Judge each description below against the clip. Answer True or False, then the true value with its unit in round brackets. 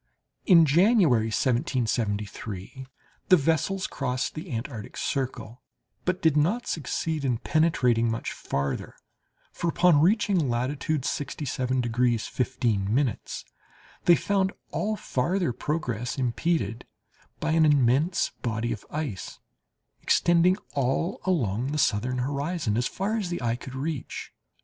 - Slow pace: True (120 wpm)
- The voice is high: False (135 Hz)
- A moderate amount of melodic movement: False (5.7 semitones)